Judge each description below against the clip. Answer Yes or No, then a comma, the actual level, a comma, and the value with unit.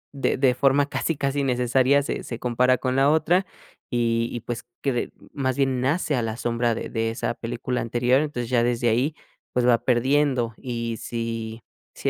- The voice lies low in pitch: Yes, low, 125 Hz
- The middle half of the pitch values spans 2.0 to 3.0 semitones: Yes, narrow, 2.6 semitones